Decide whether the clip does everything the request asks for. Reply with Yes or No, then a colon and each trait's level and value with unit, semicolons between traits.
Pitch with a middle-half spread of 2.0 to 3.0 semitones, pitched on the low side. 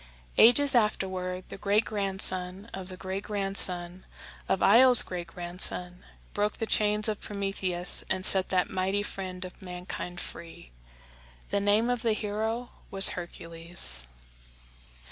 No: narrow, 2.5 semitones; high, 190 Hz